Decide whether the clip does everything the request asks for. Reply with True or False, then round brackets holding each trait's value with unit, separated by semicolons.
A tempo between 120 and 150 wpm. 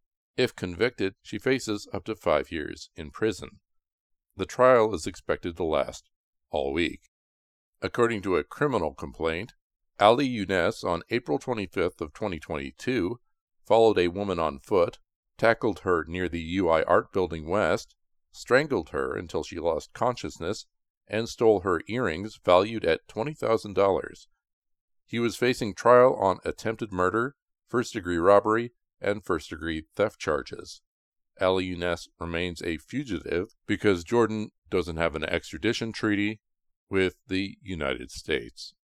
True (140 wpm)